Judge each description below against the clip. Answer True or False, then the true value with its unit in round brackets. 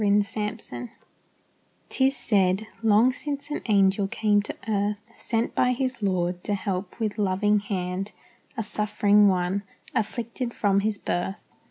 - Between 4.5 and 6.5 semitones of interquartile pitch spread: False (2.4 semitones)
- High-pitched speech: True (205 Hz)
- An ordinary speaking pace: True (145 wpm)